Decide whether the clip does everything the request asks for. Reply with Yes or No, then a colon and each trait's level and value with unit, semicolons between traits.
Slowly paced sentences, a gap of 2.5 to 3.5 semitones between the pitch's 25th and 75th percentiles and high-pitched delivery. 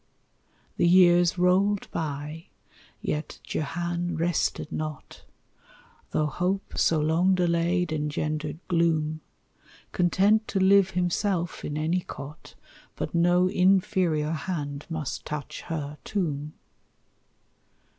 No: slow, 100 wpm; average, 2.9 semitones; medium, 170 Hz